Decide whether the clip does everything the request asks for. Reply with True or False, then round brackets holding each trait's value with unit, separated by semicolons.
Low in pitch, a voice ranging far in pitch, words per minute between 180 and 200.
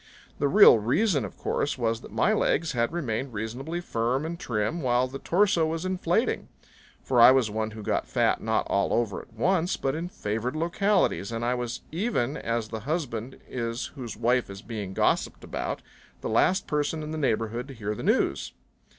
True (125 Hz; 6.0 semitones; 190 wpm)